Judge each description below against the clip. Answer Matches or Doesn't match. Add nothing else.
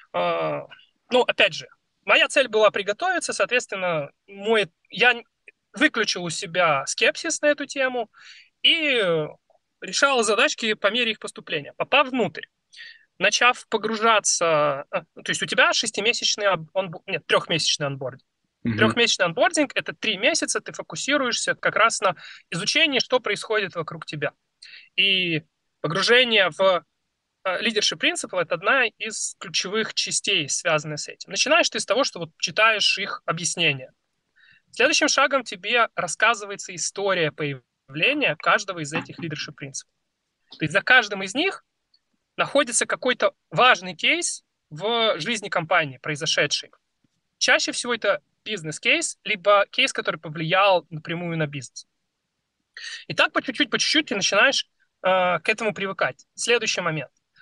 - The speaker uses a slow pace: Doesn't match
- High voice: Matches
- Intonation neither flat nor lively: Doesn't match